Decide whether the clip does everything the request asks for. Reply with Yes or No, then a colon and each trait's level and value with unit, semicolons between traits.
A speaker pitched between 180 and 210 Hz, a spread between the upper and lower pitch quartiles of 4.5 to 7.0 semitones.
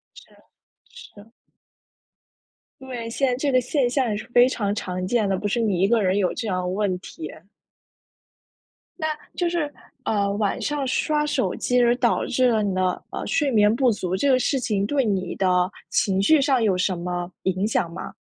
No: high, 220 Hz; average, 5.0 semitones